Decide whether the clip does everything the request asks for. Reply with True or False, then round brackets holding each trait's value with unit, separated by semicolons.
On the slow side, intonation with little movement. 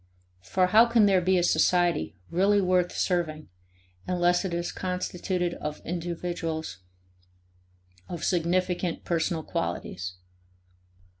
True (105 wpm; 1.6 semitones)